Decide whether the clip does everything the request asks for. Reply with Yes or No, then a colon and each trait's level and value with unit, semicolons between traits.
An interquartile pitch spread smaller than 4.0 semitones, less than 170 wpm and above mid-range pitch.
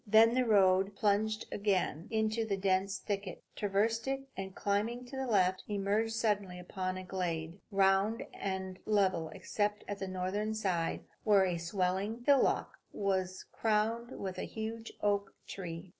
Yes: narrow, 2.6 semitones; average, 150 wpm; high, 200 Hz